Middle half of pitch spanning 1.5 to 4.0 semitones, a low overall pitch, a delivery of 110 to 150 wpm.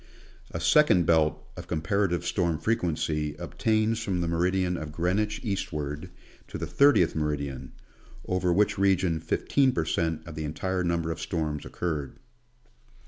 Yes: average, 3.5 semitones; very low, 85 Hz; average, 140 wpm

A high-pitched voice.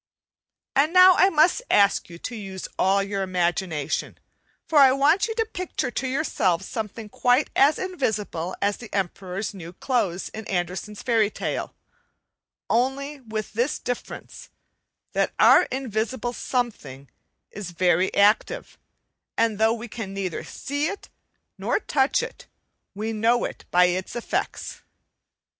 Yes: high, 220 Hz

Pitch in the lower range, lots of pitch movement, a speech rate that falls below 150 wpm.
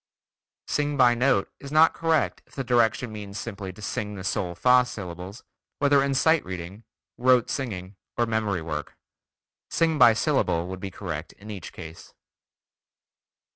No: low, 110 Hz; wide, 5.9 semitones; average, 155 wpm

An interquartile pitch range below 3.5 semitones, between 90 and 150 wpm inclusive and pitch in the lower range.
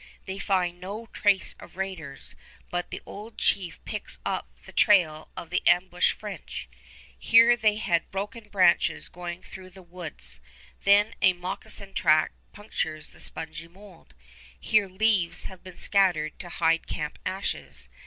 No: average, 2.8 semitones; average, 145 wpm; medium, 185 Hz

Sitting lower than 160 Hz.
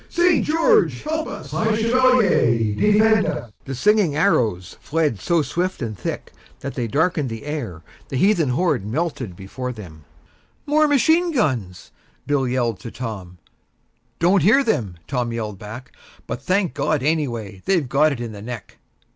Yes: medium, 140 Hz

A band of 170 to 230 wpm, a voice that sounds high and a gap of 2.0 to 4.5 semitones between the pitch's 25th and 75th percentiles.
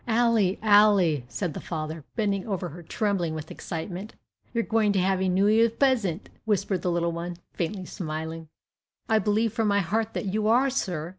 Yes: average, 190 wpm; high, 195 Hz; average, 4.2 semitones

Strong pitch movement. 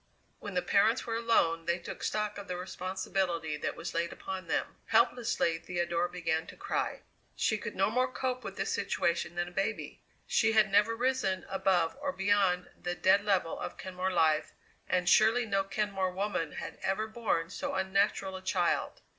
No: average, 3.3 semitones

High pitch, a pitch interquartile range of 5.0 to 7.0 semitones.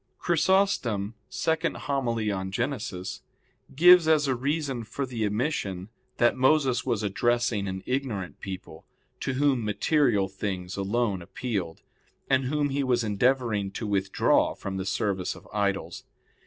No: low, 120 Hz; wide, 5.5 semitones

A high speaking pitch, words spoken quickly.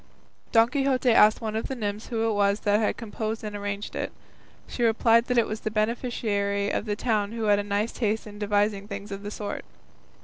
Yes: high, 215 Hz; fast, 215 wpm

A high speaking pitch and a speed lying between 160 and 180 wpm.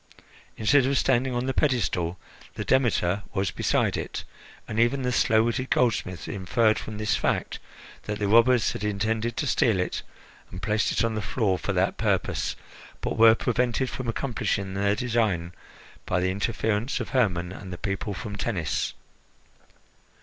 No: low, 110 Hz; average, 165 wpm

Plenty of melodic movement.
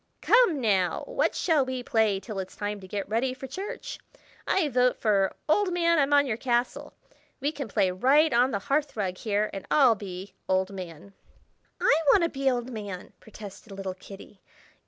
Yes: wide, 6.1 semitones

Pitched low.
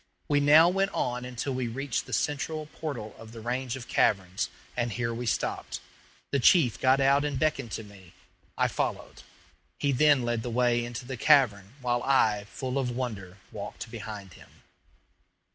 Yes: low, 125 Hz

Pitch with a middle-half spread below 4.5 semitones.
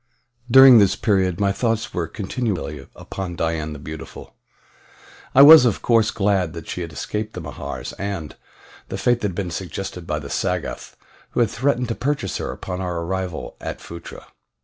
No: average, 5.1 semitones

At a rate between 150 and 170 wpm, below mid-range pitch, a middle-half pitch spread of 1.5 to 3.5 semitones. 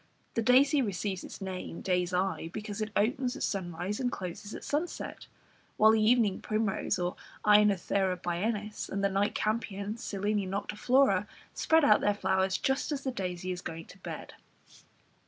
No: average, 155 wpm; high, 205 Hz; average, 3.0 semitones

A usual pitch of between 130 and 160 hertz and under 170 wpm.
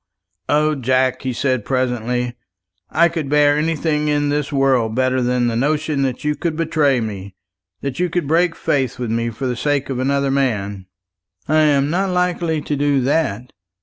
No: medium, 140 Hz; average, 180 wpm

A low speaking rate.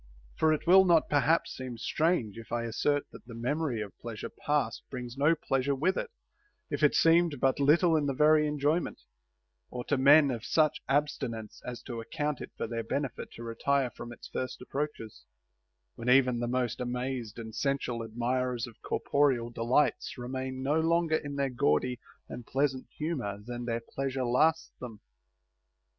No: average, 175 wpm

